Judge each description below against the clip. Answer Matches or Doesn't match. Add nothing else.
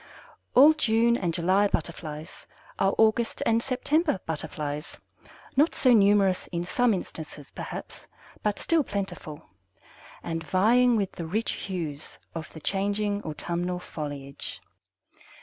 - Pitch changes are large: Matches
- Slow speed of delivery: Matches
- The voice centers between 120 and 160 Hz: Doesn't match